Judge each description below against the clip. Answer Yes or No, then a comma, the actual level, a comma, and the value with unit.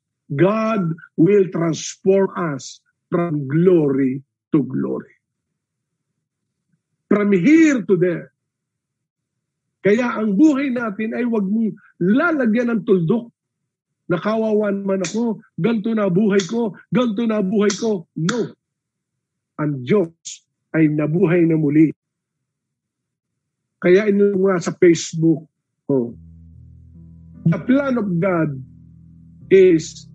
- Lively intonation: Yes, wide, 6.0 semitones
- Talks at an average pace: No, slow, 100 wpm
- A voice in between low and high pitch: Yes, medium, 175 Hz